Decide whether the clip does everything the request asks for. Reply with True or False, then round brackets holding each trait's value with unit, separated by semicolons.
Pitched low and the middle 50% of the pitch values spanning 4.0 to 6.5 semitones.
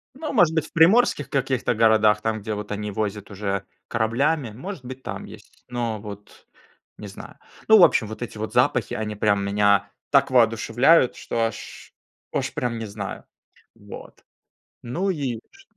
True (115 Hz; 4.6 semitones)